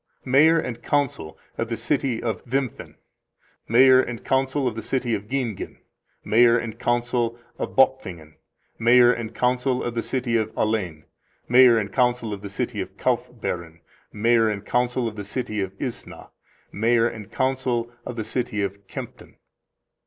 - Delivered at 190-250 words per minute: No, average, 160 wpm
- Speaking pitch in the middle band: No, low, 120 Hz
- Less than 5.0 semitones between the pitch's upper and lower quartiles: Yes, average, 2.7 semitones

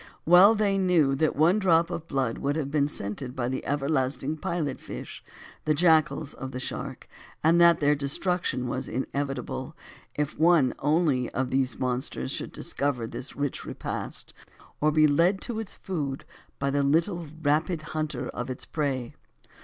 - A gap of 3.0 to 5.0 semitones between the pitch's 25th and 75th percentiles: Yes, average, 3.9 semitones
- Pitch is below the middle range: No, medium, 145 Hz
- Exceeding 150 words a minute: Yes, average, 160 wpm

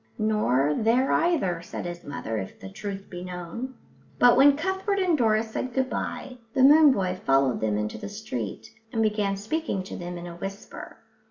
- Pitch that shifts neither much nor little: No, wide, 6.9 semitones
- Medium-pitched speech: No, high, 210 Hz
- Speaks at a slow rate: No, average, 185 wpm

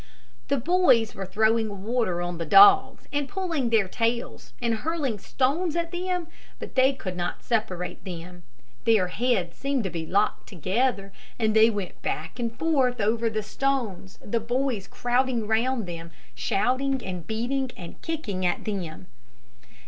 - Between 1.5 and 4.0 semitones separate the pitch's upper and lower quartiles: No, wide, 5.4 semitones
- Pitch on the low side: No, high, 230 Hz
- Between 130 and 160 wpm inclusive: Yes, average, 150 wpm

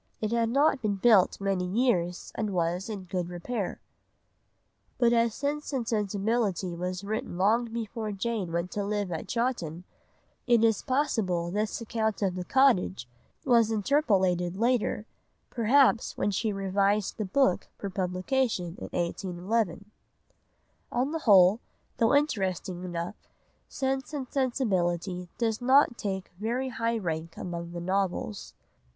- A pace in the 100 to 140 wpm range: Yes, slow, 135 wpm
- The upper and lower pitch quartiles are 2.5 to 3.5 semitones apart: No, average, 4.5 semitones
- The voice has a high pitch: Yes, high, 205 Hz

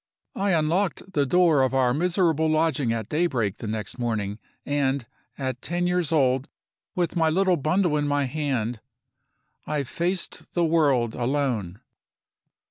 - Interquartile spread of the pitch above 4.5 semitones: Yes, average, 5.1 semitones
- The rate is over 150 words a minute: No, average, 140 wpm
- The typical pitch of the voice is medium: Yes, medium, 145 Hz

